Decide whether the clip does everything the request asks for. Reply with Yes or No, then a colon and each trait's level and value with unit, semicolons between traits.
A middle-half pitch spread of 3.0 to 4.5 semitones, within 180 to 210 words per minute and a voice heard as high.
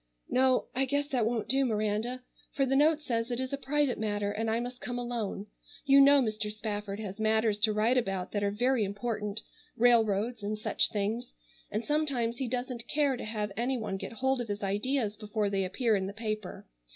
Yes: average, 3.4 semitones; fast, 205 wpm; high, 225 Hz